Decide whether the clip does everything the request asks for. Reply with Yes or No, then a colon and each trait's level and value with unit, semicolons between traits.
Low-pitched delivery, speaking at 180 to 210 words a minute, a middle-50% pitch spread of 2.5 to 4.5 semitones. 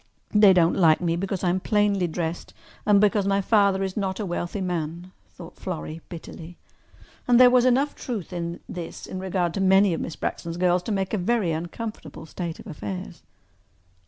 No: medium, 185 Hz; average, 190 wpm; average, 2.9 semitones